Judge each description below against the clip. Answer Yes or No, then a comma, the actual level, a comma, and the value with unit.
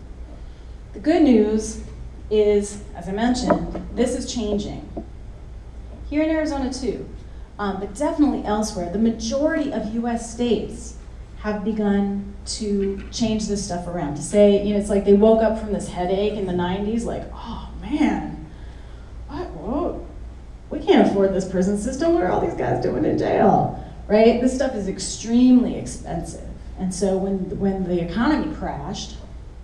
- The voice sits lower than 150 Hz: No, high, 210 Hz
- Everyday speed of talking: Yes, average, 155 wpm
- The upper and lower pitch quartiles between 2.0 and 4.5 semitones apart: Yes, average, 3.6 semitones